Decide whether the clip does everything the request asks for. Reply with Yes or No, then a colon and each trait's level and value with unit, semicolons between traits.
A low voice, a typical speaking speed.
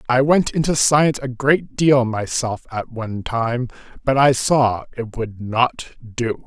Yes: low, 125 Hz; average, 165 wpm